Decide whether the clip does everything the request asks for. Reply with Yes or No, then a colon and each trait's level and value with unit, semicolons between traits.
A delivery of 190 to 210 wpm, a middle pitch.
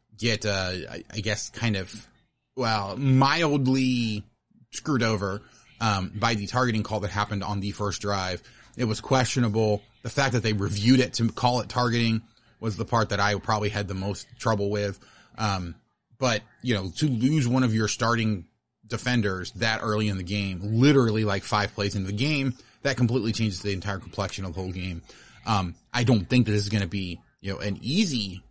No: average, 195 wpm; low, 110 Hz